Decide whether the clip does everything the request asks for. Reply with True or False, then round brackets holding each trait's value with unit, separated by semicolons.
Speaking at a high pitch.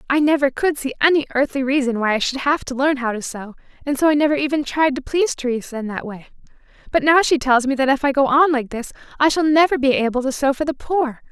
True (275 Hz)